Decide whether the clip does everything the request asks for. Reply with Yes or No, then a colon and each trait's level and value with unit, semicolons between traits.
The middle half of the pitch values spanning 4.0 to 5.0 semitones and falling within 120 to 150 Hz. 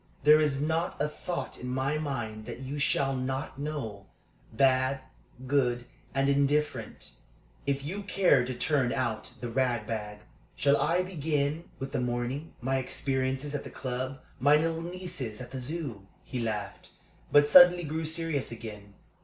No: average, 3.5 semitones; low, 135 Hz